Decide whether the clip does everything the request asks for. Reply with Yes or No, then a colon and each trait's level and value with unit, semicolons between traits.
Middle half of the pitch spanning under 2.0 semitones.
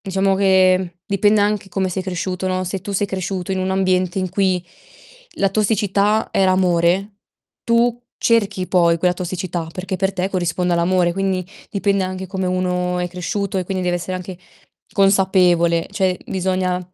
Yes: narrow, 1.4 semitones